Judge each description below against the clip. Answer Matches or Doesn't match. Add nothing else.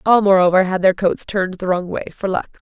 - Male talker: Doesn't match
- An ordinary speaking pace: Doesn't match